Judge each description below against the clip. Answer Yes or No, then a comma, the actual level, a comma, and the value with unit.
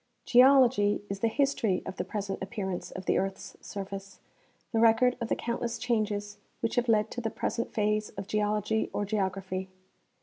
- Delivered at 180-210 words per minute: No, average, 170 wpm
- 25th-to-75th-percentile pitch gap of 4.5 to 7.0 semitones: No, average, 2.8 semitones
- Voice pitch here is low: No, high, 210 Hz